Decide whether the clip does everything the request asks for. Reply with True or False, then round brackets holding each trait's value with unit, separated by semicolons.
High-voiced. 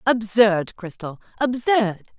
True (215 Hz)